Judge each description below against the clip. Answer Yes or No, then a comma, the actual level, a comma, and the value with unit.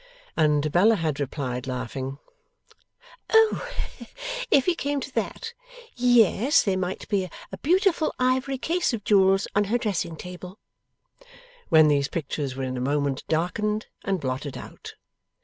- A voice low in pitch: No, medium, 185 Hz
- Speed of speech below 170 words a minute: Yes, average, 140 wpm